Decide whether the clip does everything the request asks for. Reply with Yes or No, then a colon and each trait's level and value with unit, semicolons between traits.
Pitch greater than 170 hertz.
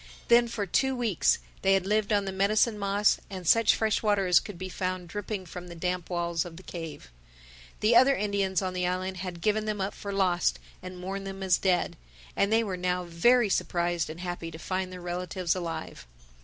Yes: medium, 185 Hz